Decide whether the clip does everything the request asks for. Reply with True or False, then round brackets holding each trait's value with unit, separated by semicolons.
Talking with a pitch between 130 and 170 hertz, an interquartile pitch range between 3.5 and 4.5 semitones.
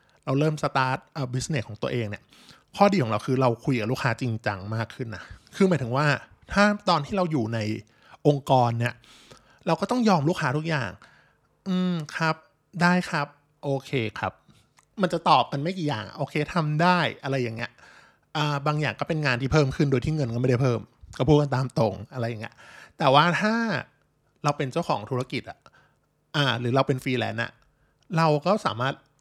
True (140 Hz; 4.2 semitones)